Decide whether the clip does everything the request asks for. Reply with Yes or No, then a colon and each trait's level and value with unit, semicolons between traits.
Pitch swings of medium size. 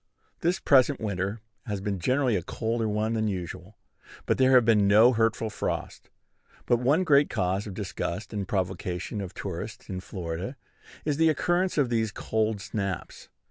Yes: average, 4.2 semitones